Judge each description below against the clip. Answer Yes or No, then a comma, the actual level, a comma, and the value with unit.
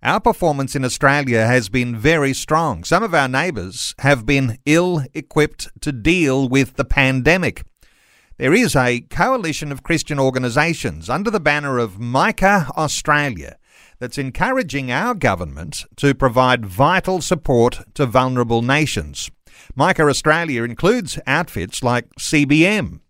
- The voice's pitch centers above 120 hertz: Yes, medium, 140 Hz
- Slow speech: Yes, slow, 130 wpm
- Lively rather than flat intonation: No, average, 4.2 semitones